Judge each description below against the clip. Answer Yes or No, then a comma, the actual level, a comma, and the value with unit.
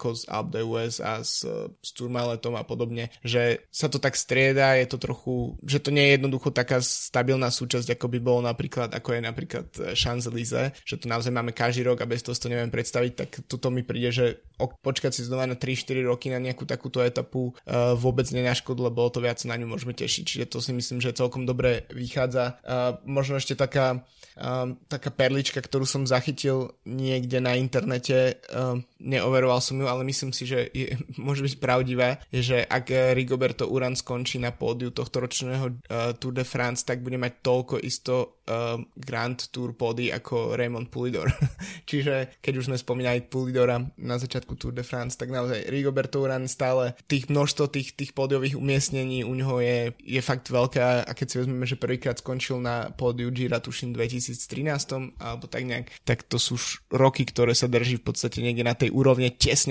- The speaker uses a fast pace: Yes, fast, 185 wpm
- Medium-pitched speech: No, low, 125 Hz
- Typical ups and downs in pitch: No, narrow, 1.4 semitones